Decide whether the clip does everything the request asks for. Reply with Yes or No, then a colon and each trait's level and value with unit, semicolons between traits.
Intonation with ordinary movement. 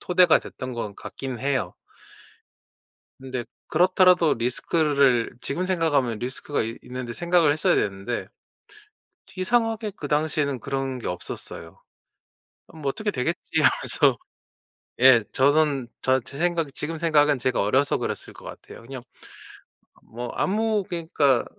Yes: average, 5.0 semitones